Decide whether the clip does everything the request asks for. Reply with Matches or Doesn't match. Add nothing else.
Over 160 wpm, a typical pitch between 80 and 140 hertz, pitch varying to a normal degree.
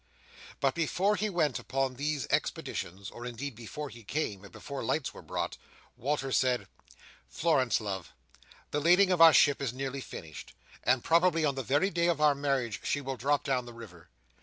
Matches